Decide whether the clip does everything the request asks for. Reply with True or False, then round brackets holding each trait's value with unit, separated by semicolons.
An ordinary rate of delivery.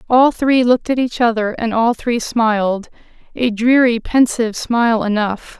True (150 wpm)